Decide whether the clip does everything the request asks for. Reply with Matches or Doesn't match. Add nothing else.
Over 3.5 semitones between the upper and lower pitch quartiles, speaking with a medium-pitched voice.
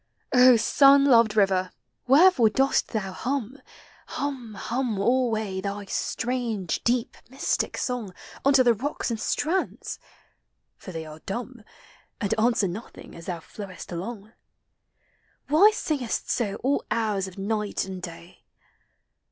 Doesn't match